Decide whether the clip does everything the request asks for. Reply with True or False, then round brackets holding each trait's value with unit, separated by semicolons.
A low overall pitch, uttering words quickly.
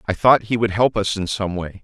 True (100 Hz; 295 wpm)